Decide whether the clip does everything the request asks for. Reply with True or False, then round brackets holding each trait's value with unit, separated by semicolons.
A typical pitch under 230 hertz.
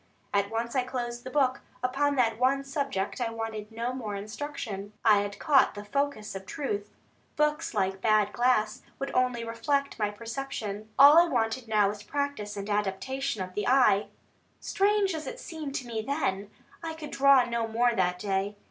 False (235 Hz)